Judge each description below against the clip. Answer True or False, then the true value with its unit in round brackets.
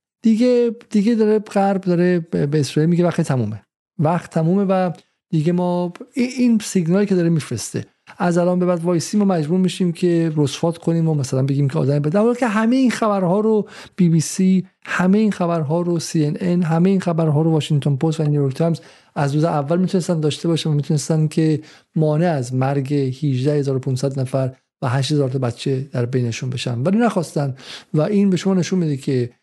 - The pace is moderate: False (185 wpm)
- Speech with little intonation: False (4.3 semitones)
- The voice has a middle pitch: True (165 Hz)